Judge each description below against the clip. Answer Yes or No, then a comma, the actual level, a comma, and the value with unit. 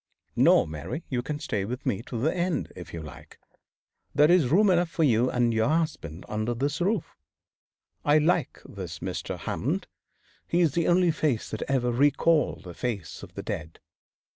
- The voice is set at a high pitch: No, low, 135 Hz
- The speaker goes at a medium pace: Yes, average, 180 wpm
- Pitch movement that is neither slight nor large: No, wide, 7.2 semitones